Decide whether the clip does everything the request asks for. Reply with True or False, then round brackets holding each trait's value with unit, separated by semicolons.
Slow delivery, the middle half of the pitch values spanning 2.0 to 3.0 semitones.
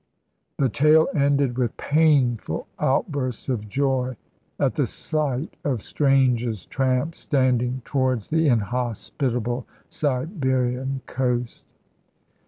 True (95 wpm; 2.5 semitones)